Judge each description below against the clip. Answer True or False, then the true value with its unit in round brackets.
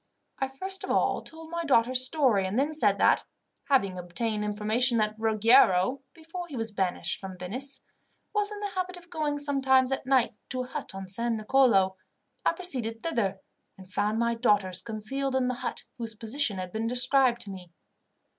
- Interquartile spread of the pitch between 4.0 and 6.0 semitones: True (4.7 semitones)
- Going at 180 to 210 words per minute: True (185 wpm)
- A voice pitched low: False (240 Hz)